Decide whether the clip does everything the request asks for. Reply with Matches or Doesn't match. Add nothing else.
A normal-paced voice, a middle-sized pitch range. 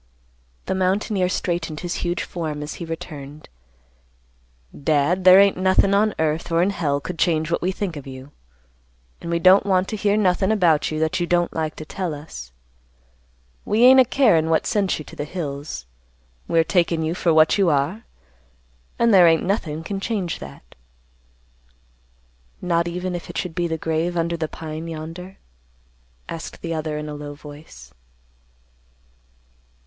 Matches